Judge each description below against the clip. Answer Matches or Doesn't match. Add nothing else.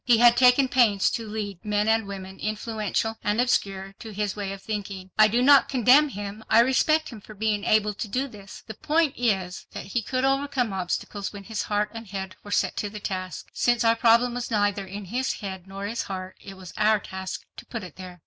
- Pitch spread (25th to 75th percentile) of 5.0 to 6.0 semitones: Doesn't match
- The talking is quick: Matches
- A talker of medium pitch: Doesn't match